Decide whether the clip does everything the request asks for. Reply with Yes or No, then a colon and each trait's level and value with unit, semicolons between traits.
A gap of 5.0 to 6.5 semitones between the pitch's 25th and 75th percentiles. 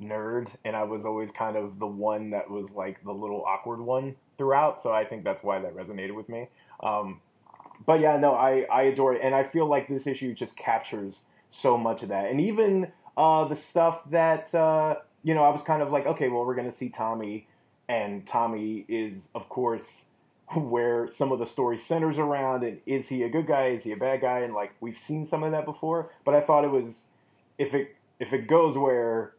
Yes: wide, 5.4 semitones